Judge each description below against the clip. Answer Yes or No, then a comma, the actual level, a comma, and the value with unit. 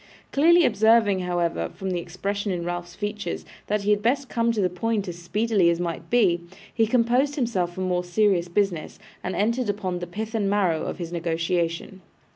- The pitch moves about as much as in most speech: Yes, average, 4.1 semitones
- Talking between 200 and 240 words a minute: No, average, 190 wpm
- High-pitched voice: Yes, high, 195 Hz